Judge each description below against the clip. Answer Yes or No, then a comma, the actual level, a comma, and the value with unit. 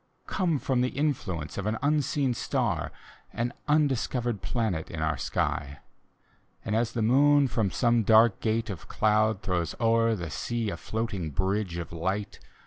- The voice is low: Yes, low, 110 Hz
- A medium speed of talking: Yes, average, 155 wpm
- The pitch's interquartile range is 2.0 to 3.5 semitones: No, average, 4.5 semitones